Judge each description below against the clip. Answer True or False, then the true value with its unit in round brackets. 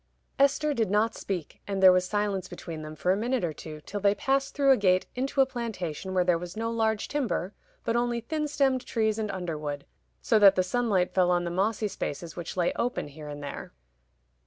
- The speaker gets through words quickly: True (215 wpm)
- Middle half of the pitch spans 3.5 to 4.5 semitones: False (5.0 semitones)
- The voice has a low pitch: False (200 Hz)